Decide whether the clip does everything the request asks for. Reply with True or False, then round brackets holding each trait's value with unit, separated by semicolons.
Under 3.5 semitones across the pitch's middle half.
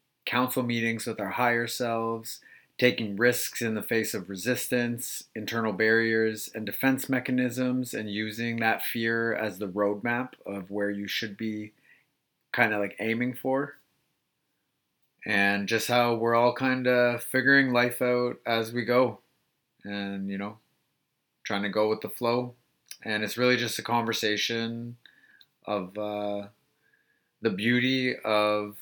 True (2.6 semitones)